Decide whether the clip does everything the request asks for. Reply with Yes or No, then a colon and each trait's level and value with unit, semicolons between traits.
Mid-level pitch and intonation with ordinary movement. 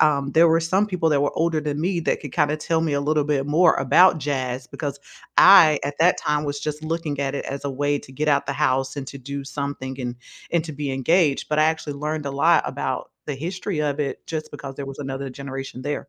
No: medium, 145 Hz; narrow, 2.3 semitones